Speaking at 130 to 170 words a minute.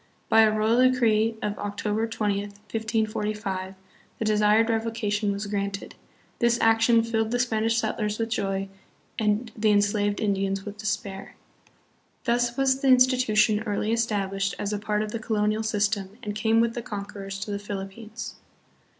Yes: average, 160 wpm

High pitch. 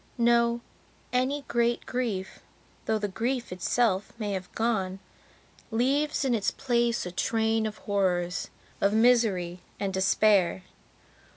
Yes: high, 220 Hz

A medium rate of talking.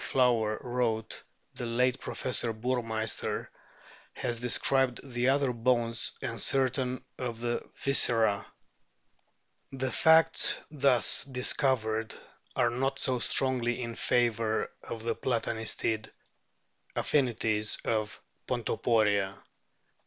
No: slow, 100 wpm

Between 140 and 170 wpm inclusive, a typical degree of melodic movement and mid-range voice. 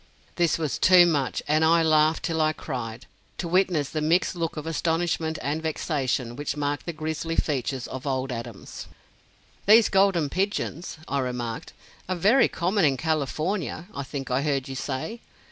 Yes: average, 165 wpm; average, 3.8 semitones; medium, 155 Hz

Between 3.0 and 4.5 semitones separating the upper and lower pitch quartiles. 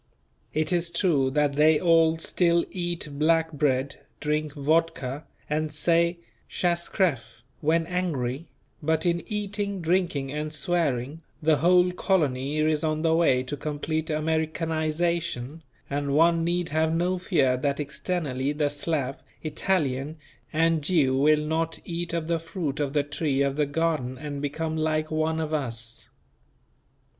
No: narrow, 2.6 semitones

